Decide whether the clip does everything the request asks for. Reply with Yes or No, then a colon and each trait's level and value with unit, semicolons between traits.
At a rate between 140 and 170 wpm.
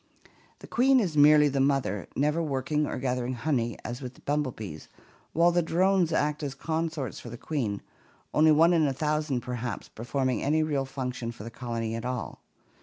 No: average, 180 wpm